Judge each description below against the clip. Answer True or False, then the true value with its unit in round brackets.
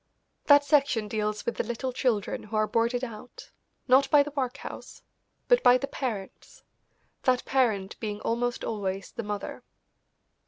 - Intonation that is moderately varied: True (3.8 semitones)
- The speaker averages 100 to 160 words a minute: True (150 wpm)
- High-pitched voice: True (240 Hz)